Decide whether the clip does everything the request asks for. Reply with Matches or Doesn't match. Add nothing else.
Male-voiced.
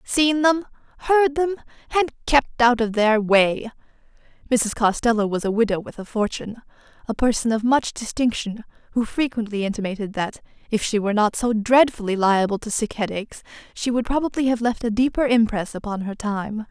Doesn't match